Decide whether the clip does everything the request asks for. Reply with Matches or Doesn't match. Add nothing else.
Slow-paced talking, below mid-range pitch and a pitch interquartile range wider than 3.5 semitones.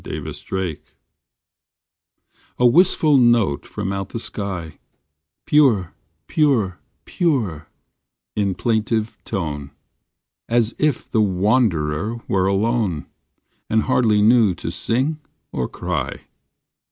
Matches